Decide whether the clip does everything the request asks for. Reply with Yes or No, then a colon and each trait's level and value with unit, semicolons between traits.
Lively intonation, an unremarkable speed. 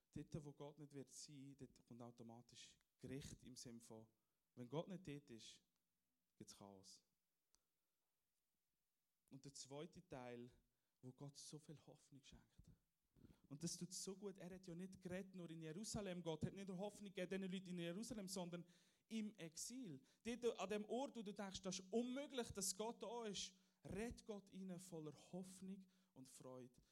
Yes: wide, 6.0 semitones; average, 170 wpm